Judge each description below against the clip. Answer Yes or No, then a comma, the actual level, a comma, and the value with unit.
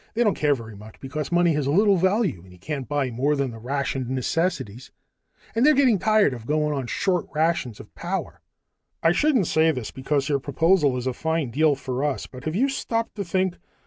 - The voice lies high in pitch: No, medium, 150 Hz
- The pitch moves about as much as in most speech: No, wide, 5.8 semitones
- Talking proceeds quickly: Yes, fast, 210 wpm